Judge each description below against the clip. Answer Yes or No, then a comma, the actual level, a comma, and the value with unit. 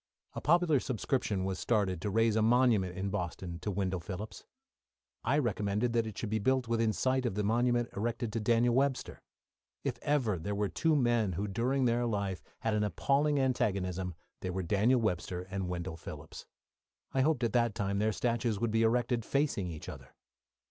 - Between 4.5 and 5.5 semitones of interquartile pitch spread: No, average, 3.7 semitones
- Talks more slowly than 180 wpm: No, average, 185 wpm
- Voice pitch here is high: No, low, 110 Hz